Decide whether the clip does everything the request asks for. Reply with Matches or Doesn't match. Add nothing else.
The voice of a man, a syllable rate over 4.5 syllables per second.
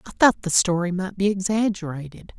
Doesn't match